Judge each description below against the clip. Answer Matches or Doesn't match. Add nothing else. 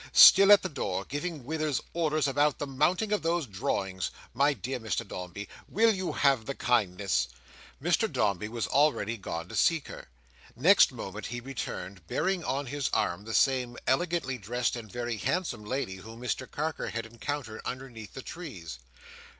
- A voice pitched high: Doesn't match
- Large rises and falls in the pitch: Matches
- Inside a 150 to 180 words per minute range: Matches